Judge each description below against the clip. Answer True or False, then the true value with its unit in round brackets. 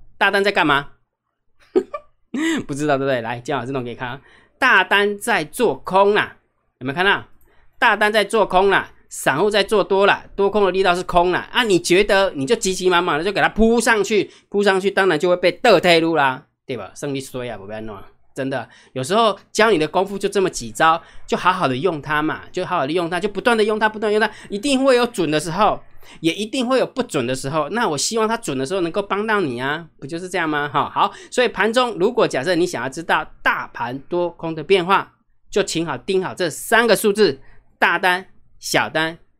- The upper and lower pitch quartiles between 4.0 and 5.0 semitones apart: False (5.4 semitones)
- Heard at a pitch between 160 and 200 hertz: True (185 Hz)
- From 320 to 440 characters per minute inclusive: False (310 characters per minute)